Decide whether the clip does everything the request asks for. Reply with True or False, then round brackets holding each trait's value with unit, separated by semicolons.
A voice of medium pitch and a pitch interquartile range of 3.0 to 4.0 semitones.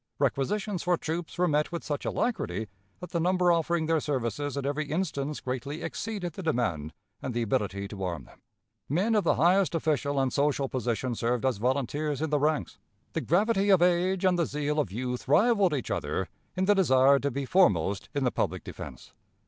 False (150 Hz; 5.4 semitones)